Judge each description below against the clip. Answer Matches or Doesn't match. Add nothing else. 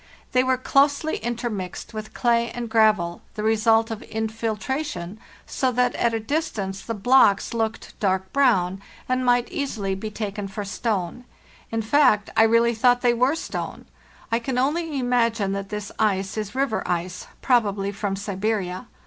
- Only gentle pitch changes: Doesn't match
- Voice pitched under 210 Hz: Doesn't match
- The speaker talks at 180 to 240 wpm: Doesn't match